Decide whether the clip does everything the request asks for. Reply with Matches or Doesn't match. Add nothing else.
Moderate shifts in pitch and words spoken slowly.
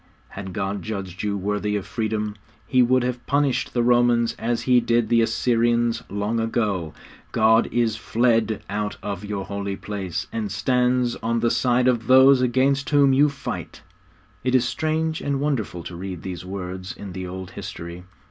Doesn't match